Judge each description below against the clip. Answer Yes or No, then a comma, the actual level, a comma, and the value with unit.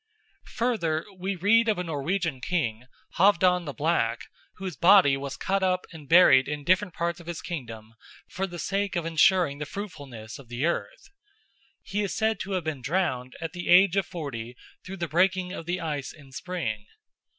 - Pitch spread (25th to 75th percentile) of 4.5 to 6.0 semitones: Yes, average, 5.0 semitones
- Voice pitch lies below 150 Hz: No, medium, 170 Hz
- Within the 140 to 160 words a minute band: No, average, 185 wpm